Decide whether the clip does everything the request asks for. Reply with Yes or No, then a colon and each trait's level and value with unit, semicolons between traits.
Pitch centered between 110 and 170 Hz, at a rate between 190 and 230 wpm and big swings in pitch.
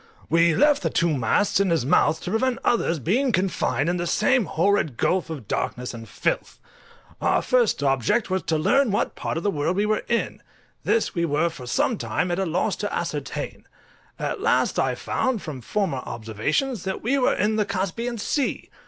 No: medium, 185 Hz; average, 195 wpm; wide, 6.5 semitones